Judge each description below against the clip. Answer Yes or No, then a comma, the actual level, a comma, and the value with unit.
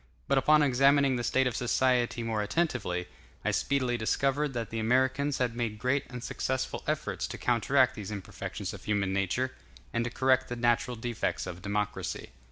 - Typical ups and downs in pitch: Yes, average, 3.1 semitones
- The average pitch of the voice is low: Yes, low, 120 Hz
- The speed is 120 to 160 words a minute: No, average, 175 wpm